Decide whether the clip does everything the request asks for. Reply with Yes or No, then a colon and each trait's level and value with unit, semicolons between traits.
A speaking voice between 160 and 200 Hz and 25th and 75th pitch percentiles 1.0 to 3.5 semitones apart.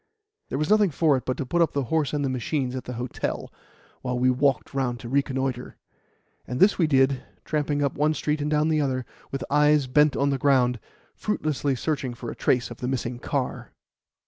No: low, 135 Hz; average, 2.8 semitones